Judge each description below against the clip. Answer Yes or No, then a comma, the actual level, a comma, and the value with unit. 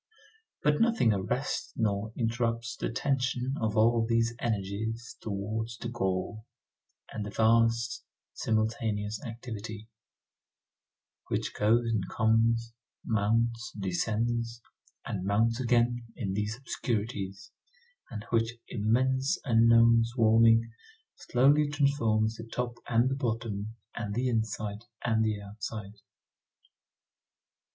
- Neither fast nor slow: No, slow, 105 wpm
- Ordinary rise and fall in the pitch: No, narrow, 1.6 semitones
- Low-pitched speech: Yes, low, 115 Hz